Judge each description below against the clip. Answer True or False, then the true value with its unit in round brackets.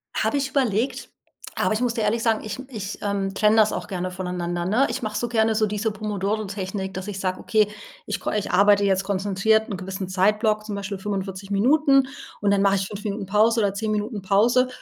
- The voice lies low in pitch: False (205 Hz)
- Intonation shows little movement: True (2.1 semitones)